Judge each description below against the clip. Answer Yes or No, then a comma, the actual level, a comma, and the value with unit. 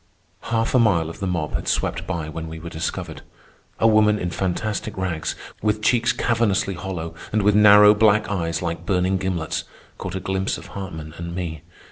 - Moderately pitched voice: No, very low, 95 Hz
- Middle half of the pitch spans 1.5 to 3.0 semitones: No, average, 4.0 semitones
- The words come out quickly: No, average, 185 wpm